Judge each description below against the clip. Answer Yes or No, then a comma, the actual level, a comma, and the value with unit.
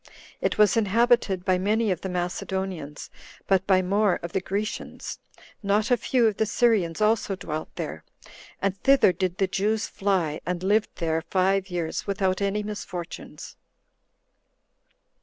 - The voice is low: No, high, 195 Hz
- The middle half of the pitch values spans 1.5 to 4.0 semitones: Yes, narrow, 2.6 semitones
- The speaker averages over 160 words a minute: No, average, 145 wpm